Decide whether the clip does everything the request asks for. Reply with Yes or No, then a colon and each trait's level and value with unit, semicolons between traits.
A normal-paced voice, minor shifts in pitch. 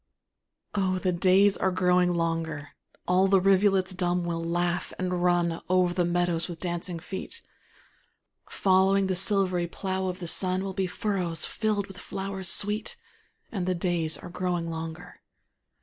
Yes: average, 155 wpm; narrow, 1.8 semitones